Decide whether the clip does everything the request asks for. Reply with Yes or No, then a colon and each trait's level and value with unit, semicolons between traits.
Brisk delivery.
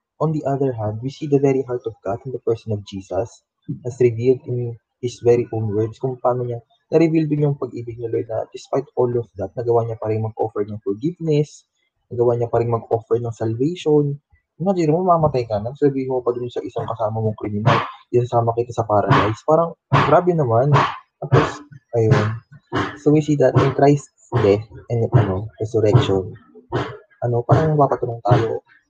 Yes: fast, 185 wpm